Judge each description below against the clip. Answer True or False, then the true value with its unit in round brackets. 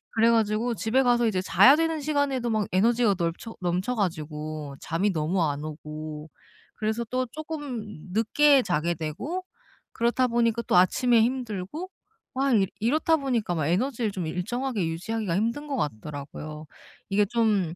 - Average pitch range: False (6.3 semitones)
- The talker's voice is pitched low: False (215 Hz)